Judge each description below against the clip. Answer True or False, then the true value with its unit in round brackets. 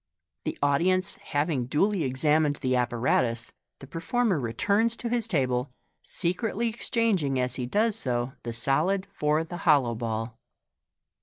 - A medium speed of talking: True (145 wpm)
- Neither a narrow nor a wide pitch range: False (7.6 semitones)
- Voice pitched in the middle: True (150 Hz)